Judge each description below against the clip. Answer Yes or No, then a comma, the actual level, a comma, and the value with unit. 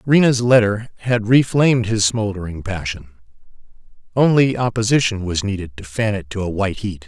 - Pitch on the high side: No, low, 110 Hz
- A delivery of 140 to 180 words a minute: Yes, average, 160 wpm